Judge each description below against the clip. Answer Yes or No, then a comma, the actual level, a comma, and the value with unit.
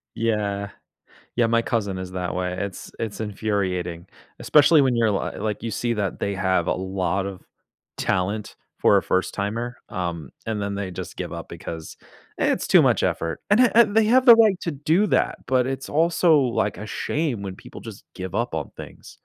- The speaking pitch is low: Yes, low, 105 Hz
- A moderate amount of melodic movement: No, wide, 6.2 semitones